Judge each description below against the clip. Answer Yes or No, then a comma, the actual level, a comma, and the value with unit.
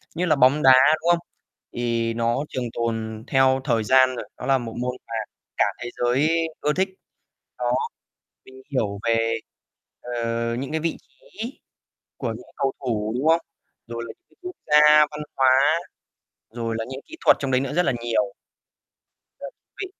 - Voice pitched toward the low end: Yes, low, 130 Hz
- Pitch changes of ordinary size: Yes, average, 4.3 semitones